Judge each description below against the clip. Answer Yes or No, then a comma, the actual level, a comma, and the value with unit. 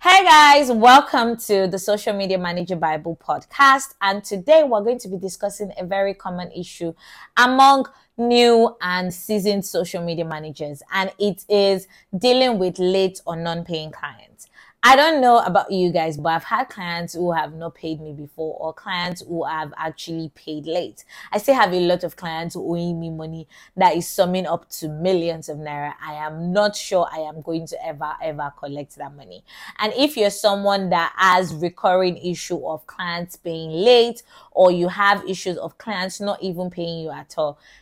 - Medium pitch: Yes, medium, 180 Hz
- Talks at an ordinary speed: Yes, average, 185 wpm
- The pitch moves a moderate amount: Yes, average, 3.7 semitones